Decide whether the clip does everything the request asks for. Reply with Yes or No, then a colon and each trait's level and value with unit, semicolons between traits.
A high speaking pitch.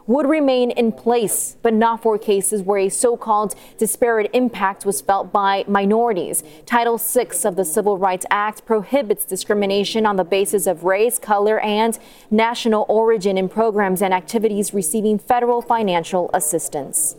Yes: high, 215 Hz